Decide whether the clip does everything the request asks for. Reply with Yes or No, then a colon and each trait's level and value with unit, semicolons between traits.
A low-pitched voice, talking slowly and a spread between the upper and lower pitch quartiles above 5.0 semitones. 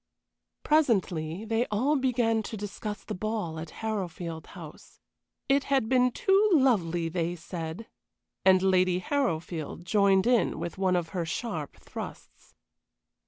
No: high, 195 Hz; slow, 130 wpm; wide, 5.6 semitones